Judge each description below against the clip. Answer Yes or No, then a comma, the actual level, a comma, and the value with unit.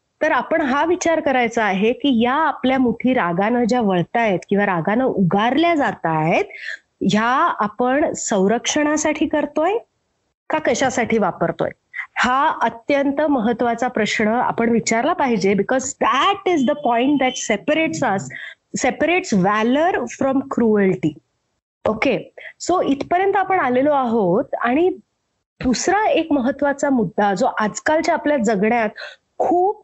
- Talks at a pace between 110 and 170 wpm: Yes, average, 120 wpm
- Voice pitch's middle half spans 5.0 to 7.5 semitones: Yes, wide, 5.4 semitones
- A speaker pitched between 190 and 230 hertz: No, very high, 255 Hz